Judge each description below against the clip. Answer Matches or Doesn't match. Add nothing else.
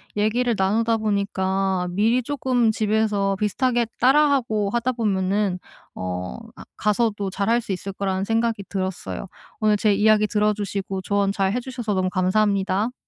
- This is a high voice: Matches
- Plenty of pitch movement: Doesn't match